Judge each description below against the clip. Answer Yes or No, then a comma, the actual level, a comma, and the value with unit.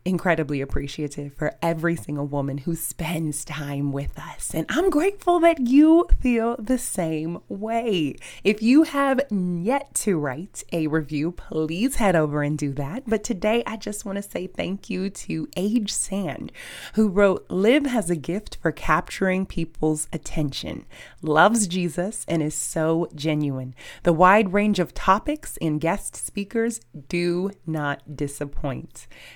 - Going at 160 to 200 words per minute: No, average, 150 wpm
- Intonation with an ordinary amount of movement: No, wide, 5.8 semitones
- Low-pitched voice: No, medium, 175 Hz